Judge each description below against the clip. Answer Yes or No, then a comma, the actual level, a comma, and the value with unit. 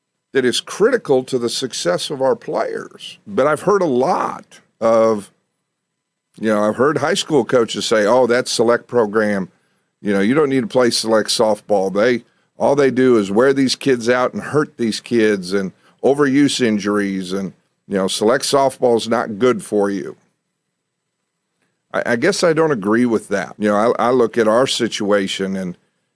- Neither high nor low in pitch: No, low, 110 Hz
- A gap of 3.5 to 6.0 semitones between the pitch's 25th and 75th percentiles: Yes, average, 4.1 semitones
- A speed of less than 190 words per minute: Yes, average, 180 wpm